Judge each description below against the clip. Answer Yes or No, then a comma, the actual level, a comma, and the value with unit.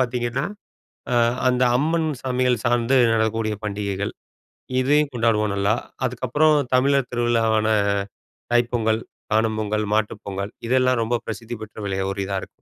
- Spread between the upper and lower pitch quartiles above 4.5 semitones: No, average, 2.9 semitones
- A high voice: No, low, 115 Hz